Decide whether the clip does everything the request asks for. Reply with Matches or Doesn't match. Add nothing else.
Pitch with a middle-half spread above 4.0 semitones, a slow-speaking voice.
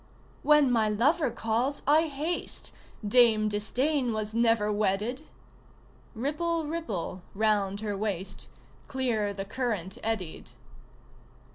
Matches